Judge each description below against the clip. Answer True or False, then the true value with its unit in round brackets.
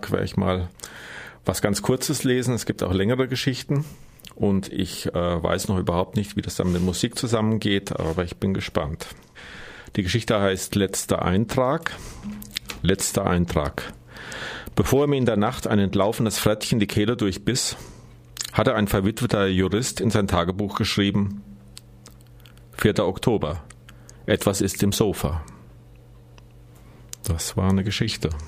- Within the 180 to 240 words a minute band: False (140 wpm)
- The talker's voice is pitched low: True (100 Hz)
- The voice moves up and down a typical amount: True (3.7 semitones)